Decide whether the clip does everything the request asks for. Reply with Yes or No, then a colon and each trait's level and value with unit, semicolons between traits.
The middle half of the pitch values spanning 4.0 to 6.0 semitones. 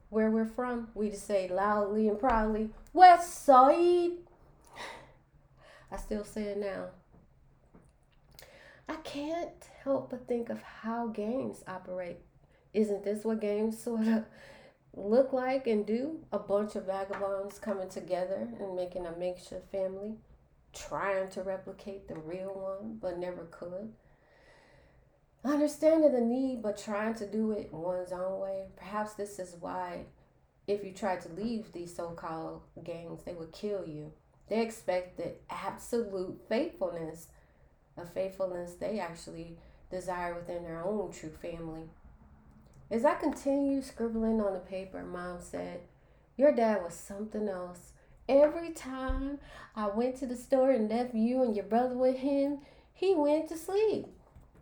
Yes: average, 5.1 semitones